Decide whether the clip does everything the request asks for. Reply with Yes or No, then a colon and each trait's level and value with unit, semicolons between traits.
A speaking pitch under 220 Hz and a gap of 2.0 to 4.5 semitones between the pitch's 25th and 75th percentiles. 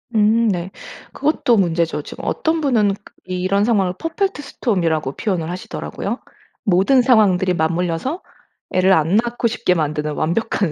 No: high, 190 Hz; wide, 5.5 semitones